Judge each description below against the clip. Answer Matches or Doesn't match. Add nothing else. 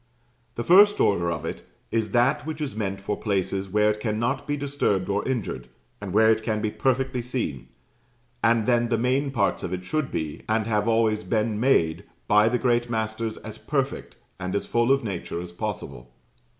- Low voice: Matches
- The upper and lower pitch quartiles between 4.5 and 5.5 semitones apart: Doesn't match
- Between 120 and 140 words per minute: Doesn't match